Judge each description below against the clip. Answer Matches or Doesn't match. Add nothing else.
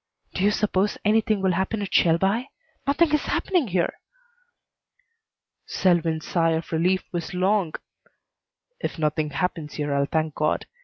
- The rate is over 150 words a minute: Doesn't match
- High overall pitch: Doesn't match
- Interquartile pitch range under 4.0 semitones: Doesn't match